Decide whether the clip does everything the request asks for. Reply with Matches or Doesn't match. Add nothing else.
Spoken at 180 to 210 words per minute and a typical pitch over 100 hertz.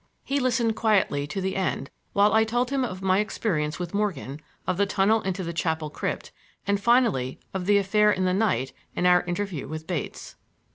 Matches